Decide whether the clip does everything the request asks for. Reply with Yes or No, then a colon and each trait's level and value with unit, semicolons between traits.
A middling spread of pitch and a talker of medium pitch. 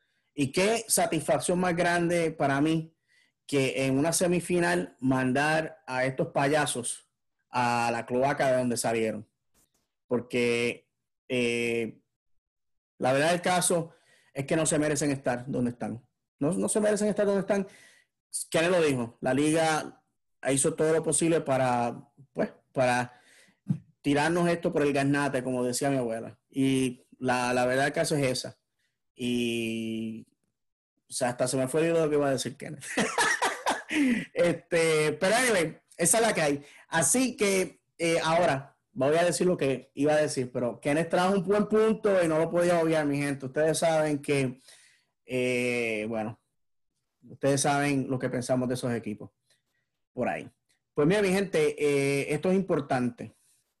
Yes: average, 4.7 semitones; medium, 145 Hz